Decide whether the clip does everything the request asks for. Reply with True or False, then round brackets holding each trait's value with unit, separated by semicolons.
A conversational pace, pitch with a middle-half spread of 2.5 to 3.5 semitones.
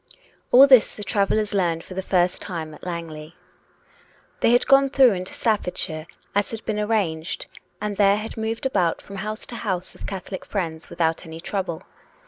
False (180 wpm; 4.2 semitones)